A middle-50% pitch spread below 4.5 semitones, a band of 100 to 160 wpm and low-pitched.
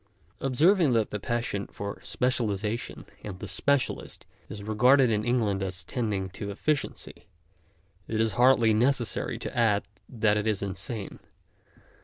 Yes: average, 3.5 semitones; average, 140 wpm; low, 110 Hz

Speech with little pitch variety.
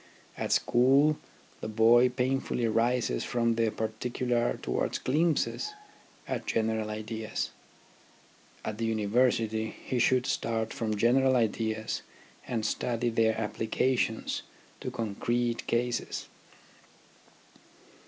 Yes: narrow, 2.0 semitones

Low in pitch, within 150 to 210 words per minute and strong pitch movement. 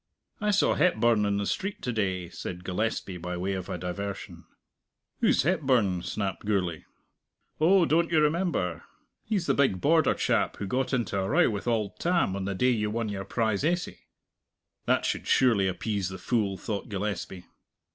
Yes: low, 105 Hz; average, 175 wpm; wide, 6.7 semitones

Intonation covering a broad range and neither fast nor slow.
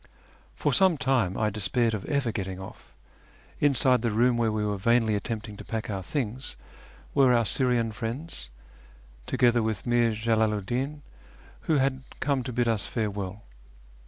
No: average, 3.2 semitones; average, 165 wpm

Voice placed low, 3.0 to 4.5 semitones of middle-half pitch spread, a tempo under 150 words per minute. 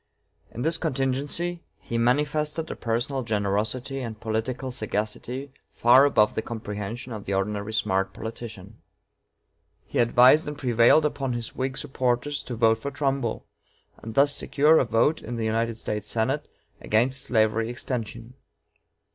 Yes: low, 120 Hz; average, 3.6 semitones; average, 140 wpm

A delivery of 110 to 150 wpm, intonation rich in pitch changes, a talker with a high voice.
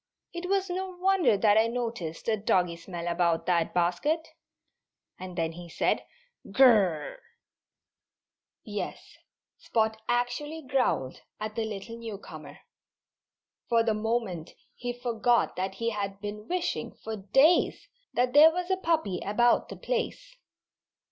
Yes: average, 140 wpm; wide, 6.7 semitones; high, 225 Hz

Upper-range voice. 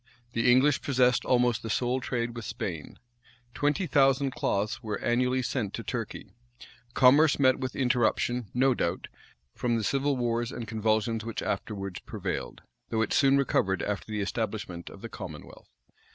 No: low, 120 Hz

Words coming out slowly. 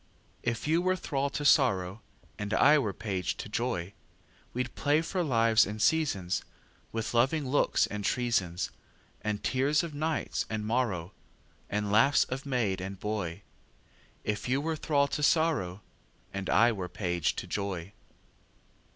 Yes: slow, 125 wpm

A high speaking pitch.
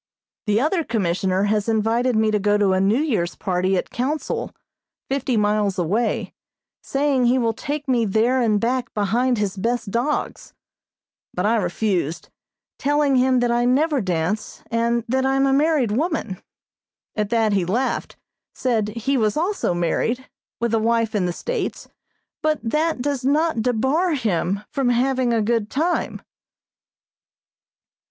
Yes: high, 235 Hz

